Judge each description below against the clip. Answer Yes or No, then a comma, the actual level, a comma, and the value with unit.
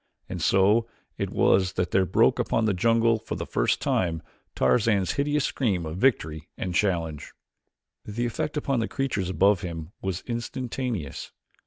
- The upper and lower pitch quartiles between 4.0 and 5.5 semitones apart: Yes, average, 4.8 semitones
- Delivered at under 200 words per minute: Yes, average, 155 wpm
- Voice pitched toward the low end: Yes, low, 100 Hz